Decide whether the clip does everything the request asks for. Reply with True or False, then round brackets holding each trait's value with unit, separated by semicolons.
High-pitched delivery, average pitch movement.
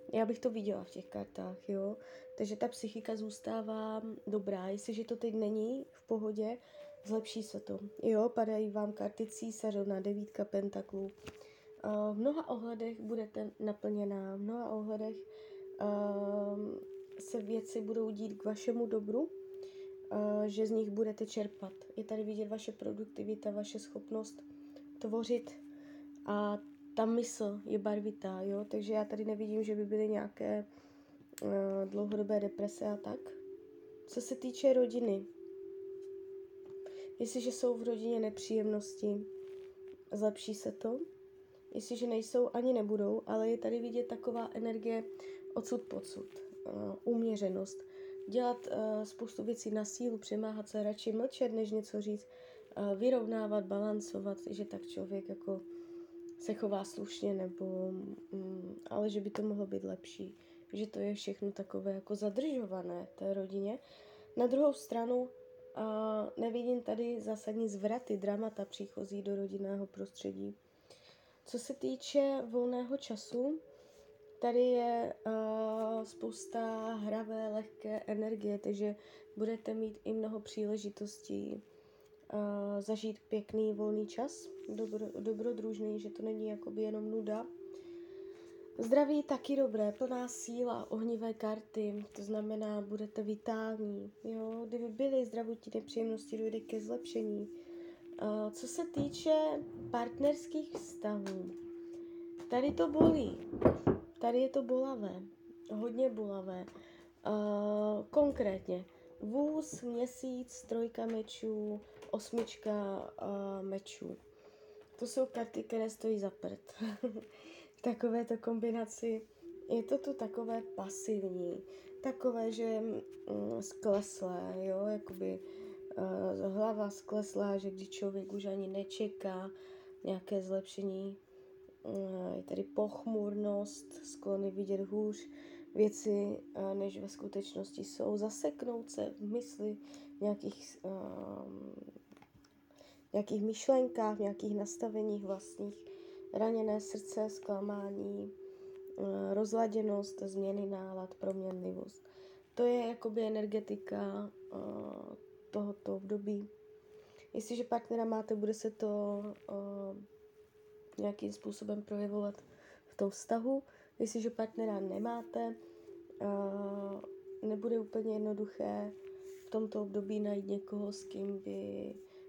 True (220 Hz; 3.7 semitones)